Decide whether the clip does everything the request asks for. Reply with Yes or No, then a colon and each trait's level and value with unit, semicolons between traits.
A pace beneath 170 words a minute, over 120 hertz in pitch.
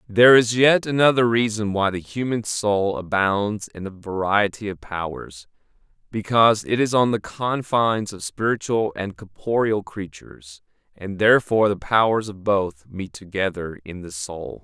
No: average, 150 wpm; low, 105 Hz